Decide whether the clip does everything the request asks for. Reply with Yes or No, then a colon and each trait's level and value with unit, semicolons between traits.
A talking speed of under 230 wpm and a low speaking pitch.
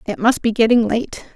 No: fast, 220 wpm; high, 230 Hz